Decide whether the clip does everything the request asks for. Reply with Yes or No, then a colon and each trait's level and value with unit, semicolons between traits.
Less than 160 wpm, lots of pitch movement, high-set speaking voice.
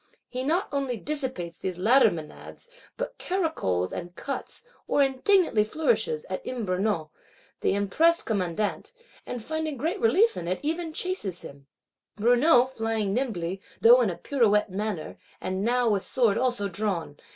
Yes: average, 150 wpm; wide, 7.8 semitones; high, 235 Hz